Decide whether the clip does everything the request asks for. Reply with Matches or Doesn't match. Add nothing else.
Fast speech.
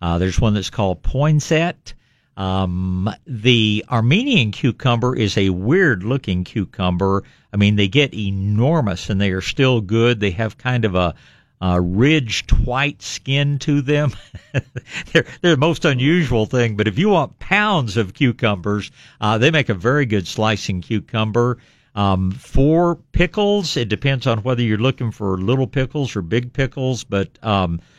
Doesn't match